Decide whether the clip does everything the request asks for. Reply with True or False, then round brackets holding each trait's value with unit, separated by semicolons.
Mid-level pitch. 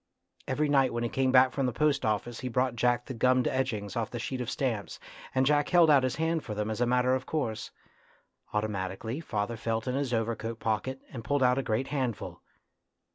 False (125 Hz)